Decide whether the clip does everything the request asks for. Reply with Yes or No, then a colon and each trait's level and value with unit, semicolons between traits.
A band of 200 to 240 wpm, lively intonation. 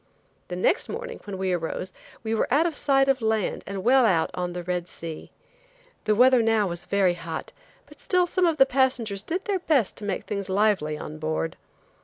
Yes: fast, 205 wpm; wide, 7.0 semitones